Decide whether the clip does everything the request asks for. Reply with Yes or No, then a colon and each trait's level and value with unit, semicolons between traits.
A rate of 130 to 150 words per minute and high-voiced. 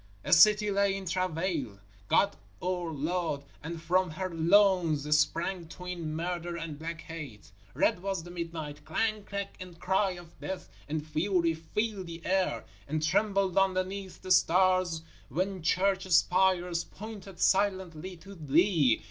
No: average, 145 wpm; medium, 180 Hz